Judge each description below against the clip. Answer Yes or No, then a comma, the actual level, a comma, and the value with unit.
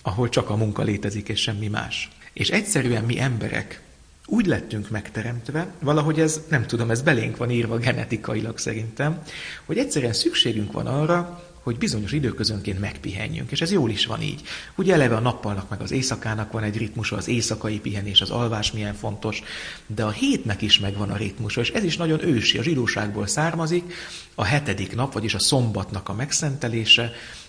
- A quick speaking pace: Yes, fast, 175 wpm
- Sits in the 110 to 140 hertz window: Yes, low, 115 Hz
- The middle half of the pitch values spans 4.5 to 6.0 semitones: Yes, average, 4.8 semitones